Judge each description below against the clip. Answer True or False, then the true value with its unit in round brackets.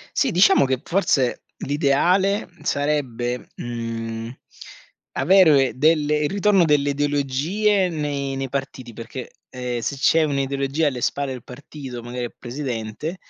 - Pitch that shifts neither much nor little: True (3.8 semitones)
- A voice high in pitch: False (140 Hz)